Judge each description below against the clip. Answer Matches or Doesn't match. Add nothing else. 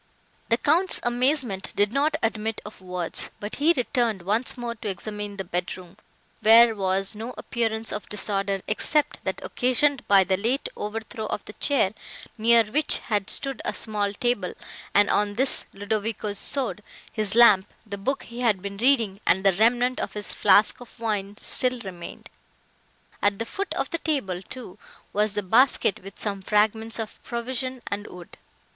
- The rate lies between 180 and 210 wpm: Doesn't match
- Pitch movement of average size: Matches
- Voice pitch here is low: Doesn't match